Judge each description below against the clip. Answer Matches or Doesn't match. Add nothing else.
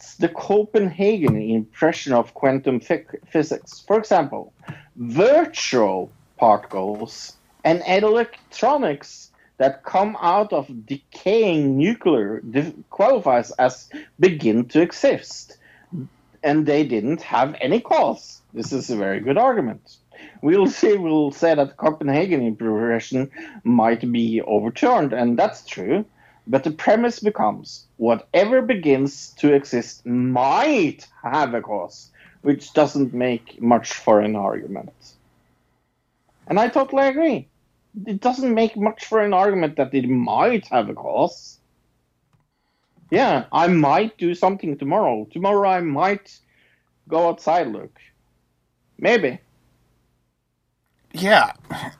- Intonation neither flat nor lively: Doesn't match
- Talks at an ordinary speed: Doesn't match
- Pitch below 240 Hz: Matches